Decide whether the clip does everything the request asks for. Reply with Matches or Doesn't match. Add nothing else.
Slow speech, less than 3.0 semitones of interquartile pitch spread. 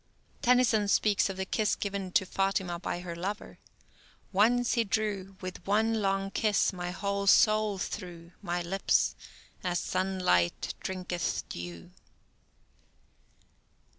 Matches